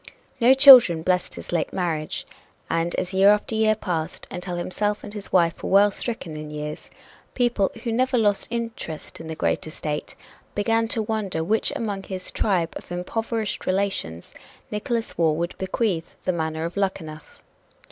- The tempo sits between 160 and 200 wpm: Yes, average, 170 wpm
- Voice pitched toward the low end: No, high, 190 Hz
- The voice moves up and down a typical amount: Yes, average, 4.8 semitones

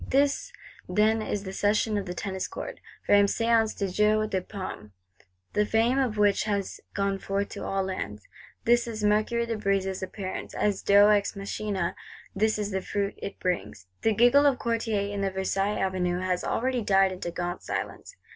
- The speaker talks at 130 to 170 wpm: No, average, 180 wpm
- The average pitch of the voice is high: Yes, high, 205 Hz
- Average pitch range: No, narrow, 2.3 semitones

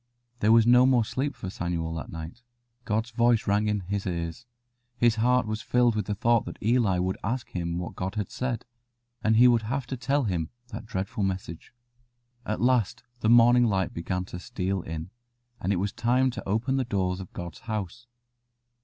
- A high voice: No, low, 110 Hz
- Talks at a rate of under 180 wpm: No, average, 195 wpm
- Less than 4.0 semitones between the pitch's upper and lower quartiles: No, average, 4.6 semitones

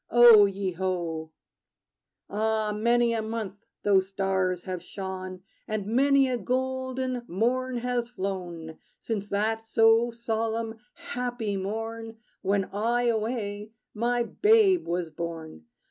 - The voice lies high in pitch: Yes, high, 220 Hz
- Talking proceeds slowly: Yes, slow, 115 wpm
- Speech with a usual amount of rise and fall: Yes, average, 3.9 semitones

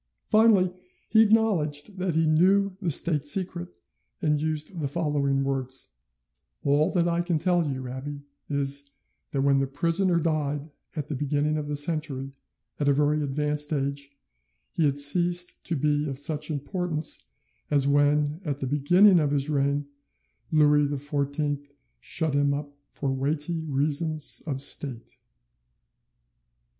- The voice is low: No, medium, 150 Hz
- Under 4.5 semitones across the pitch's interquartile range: Yes, narrow, 2.6 semitones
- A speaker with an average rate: Yes, average, 145 wpm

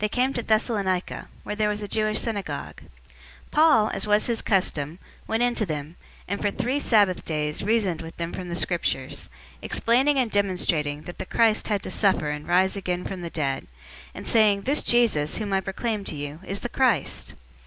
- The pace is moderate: Yes, average, 165 wpm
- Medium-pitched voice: No, high, 200 Hz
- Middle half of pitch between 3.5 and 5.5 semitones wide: Yes, average, 4.5 semitones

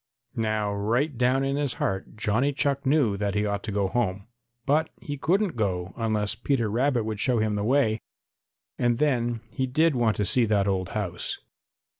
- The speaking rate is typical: Yes, average, 185 wpm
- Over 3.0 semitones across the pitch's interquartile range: Yes, average, 4.8 semitones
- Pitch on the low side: Yes, low, 115 Hz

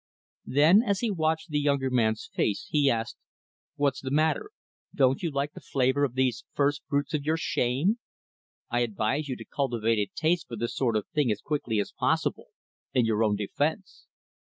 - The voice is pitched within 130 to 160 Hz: Yes, medium, 140 Hz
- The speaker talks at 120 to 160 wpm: No, average, 185 wpm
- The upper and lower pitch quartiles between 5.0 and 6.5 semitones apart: No, average, 4.4 semitones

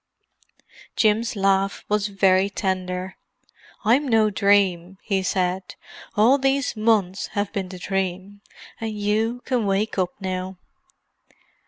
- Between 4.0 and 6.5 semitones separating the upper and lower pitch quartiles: No, narrow, 2.4 semitones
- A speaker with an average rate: No, slow, 115 wpm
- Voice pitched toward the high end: Yes, high, 200 Hz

